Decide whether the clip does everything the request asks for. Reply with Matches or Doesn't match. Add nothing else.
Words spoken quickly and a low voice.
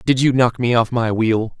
Matches